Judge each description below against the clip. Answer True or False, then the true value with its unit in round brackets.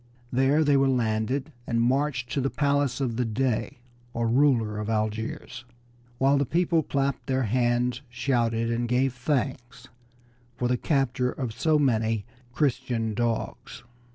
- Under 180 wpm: True (145 wpm)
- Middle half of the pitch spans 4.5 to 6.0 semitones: False (2.8 semitones)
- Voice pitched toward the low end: True (125 Hz)